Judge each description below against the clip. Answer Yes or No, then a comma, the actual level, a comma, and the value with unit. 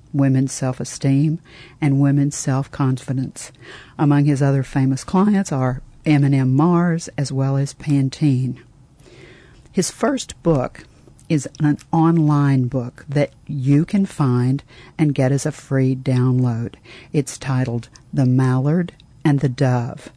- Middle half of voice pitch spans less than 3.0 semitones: Yes, narrow, 2.4 semitones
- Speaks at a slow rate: Yes, slow, 130 wpm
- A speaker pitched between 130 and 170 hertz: Yes, medium, 140 Hz